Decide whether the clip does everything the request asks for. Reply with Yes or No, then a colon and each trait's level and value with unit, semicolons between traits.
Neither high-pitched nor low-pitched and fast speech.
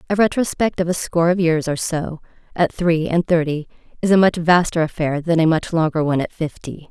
Yes: medium, 165 Hz; fast, 215 wpm